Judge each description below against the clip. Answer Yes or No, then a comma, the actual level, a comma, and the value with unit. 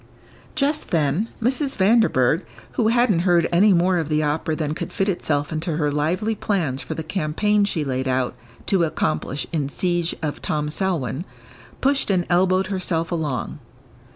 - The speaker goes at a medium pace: Yes, average, 160 wpm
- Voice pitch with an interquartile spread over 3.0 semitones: Yes, average, 4.5 semitones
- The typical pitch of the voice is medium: Yes, medium, 170 Hz